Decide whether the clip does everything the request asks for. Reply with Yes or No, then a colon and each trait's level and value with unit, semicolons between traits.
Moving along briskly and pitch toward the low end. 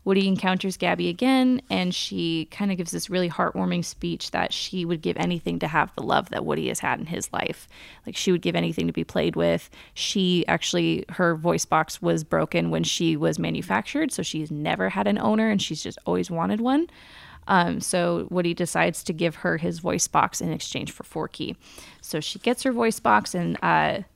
No: fast, 210 wpm; medium, 175 Hz